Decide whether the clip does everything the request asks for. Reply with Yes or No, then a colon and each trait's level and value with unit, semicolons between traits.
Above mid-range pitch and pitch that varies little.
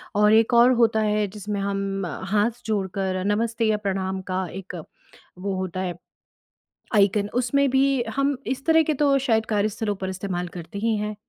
No: high, 210 Hz; average, 3.1 semitones